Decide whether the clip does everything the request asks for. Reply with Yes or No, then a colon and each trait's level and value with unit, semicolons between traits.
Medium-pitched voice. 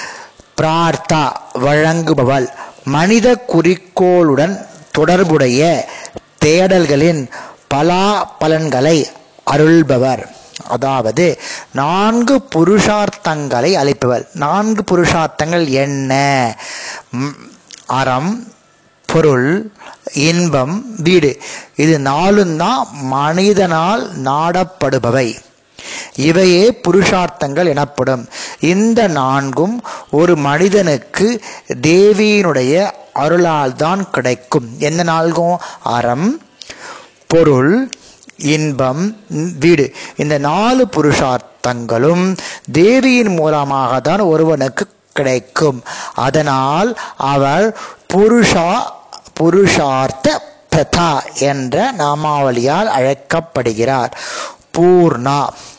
Yes: medium, 160 Hz